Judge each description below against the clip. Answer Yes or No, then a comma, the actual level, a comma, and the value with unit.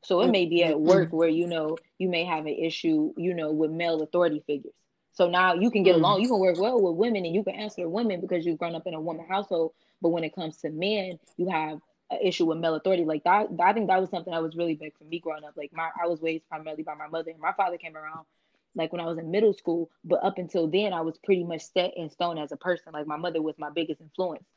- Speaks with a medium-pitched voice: Yes, medium, 170 Hz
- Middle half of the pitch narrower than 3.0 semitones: Yes, narrow, 2.4 semitones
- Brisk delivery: Yes, fast, 280 wpm